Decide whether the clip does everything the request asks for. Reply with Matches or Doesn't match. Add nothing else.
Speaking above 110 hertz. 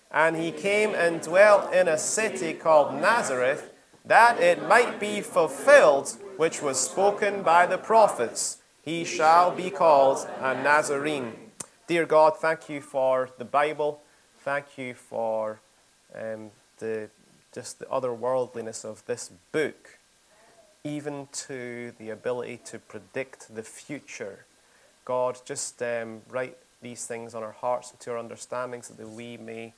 Matches